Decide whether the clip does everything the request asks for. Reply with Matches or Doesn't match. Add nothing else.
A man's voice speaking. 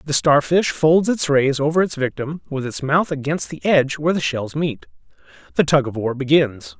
Matches